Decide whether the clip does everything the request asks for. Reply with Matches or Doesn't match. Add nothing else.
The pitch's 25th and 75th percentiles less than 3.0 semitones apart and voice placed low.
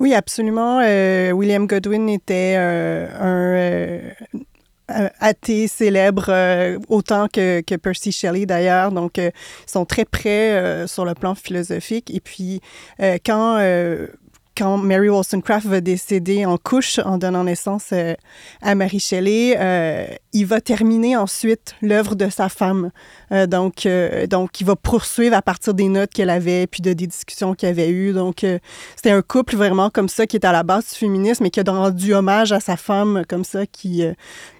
Doesn't match